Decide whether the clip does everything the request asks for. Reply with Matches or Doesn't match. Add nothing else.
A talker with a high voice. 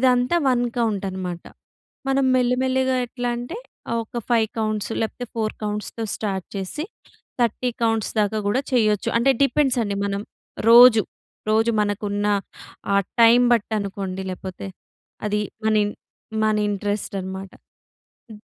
Matches